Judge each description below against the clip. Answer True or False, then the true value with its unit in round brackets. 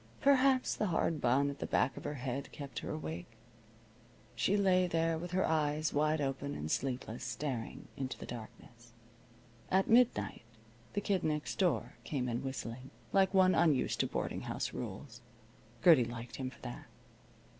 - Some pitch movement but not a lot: False (6.2 semitones)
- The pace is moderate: True (165 wpm)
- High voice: False (140 Hz)